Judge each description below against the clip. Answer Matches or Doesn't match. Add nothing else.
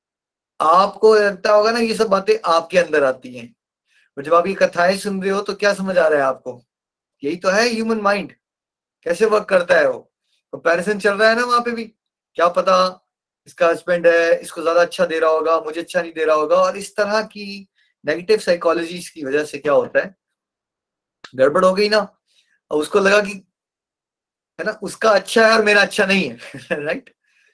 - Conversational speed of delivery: Doesn't match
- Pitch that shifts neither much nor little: Matches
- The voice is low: Doesn't match